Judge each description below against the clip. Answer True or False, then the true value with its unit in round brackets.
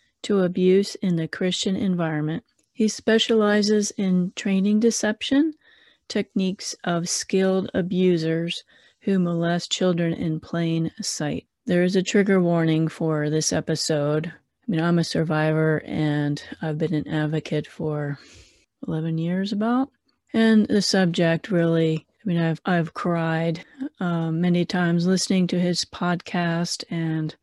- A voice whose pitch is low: False (175 Hz)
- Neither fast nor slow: False (130 wpm)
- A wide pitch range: False (3.6 semitones)